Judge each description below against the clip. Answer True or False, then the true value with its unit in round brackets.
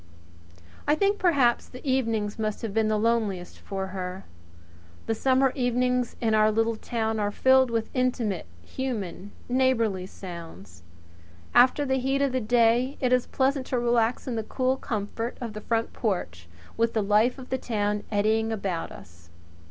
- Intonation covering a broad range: False (3.5 semitones)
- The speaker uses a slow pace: False (170 wpm)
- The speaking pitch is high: True (225 Hz)